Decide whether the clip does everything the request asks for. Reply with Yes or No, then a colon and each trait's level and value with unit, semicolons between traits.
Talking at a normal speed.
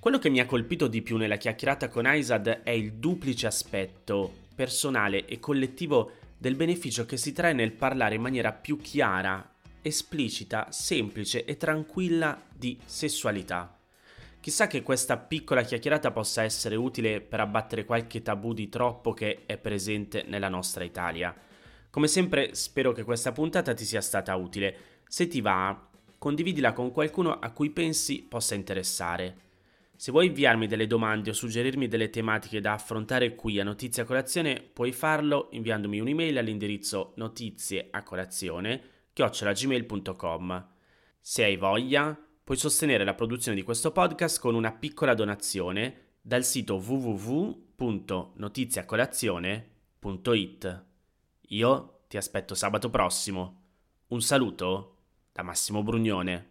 Yes: average, 135 wpm